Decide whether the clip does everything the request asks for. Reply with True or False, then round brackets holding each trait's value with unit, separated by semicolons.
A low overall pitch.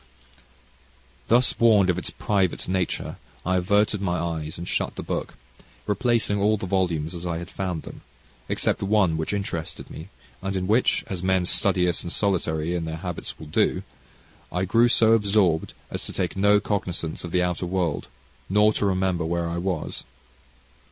True (95 Hz)